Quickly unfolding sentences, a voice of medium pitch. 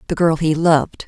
Yes: fast, 225 wpm; medium, 160 Hz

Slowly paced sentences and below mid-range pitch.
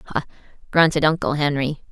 No: slow, 125 wpm; medium, 150 Hz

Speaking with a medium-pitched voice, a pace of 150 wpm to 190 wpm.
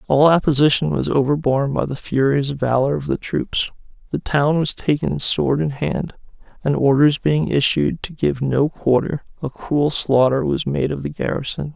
Yes: medium, 145 Hz; average, 175 wpm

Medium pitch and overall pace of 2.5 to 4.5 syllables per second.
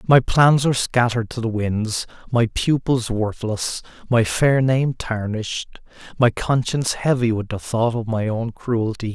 No: low, 115 Hz; 4.4 syllables/s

